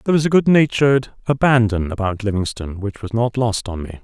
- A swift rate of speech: No, average, 195 wpm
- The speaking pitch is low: Yes, low, 115 Hz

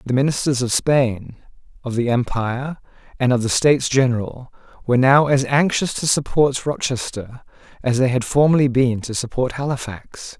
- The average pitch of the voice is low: Yes, low, 130 Hz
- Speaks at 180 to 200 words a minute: No, average, 155 wpm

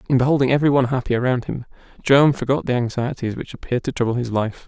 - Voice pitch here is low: Yes, low, 125 Hz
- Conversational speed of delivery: No, fast, 220 wpm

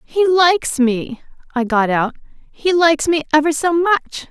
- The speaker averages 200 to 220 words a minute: No, average, 165 wpm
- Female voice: Yes, female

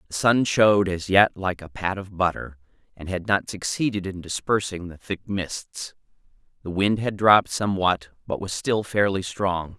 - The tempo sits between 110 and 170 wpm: No, average, 180 wpm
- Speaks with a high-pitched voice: No, very low, 95 Hz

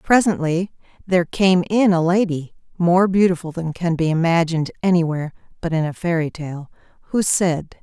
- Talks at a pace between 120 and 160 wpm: Yes, average, 155 wpm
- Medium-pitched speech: Yes, medium, 175 Hz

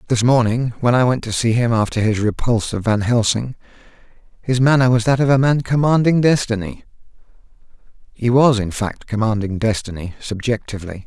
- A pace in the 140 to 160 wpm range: Yes, average, 155 wpm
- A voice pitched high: No, low, 115 Hz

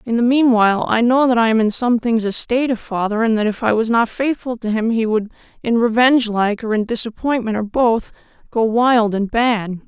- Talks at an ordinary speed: No, fast, 220 wpm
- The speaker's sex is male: No, female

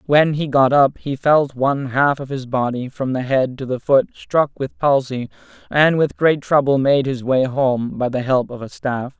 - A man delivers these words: Yes, male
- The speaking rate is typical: No, fast, 220 wpm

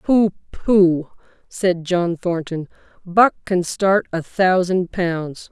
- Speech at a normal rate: No, slow, 120 wpm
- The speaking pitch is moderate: Yes, medium, 180 Hz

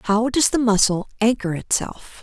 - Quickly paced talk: No, average, 160 wpm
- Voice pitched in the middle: No, high, 225 Hz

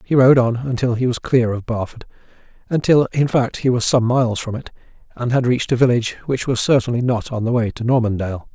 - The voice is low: Yes, low, 120 Hz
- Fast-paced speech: Yes, fast, 225 wpm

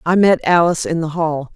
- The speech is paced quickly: Yes, fast, 230 wpm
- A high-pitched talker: No, medium, 165 Hz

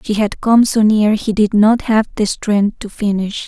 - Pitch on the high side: Yes, high, 210 Hz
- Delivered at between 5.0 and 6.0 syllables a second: No, 4.3 syllables/s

